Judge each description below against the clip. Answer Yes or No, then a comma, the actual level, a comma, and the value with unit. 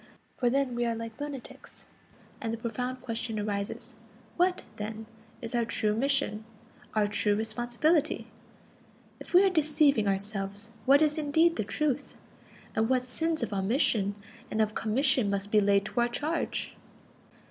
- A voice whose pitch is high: Yes, high, 235 Hz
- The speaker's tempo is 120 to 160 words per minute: Yes, average, 150 wpm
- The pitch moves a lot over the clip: No, average, 4.7 semitones